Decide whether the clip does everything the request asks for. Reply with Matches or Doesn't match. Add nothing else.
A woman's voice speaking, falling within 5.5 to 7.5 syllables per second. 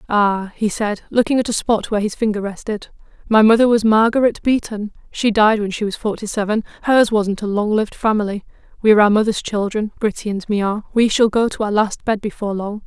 Matches